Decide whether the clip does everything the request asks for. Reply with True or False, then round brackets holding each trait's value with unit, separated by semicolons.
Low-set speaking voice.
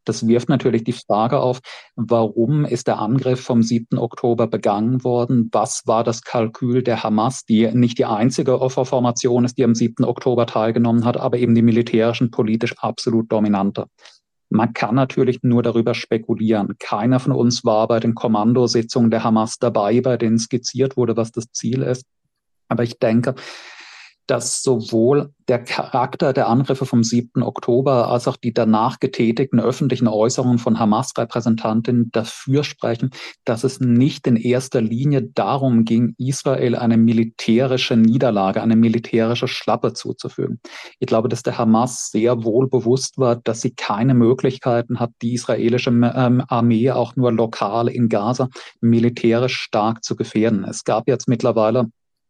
True (120 Hz)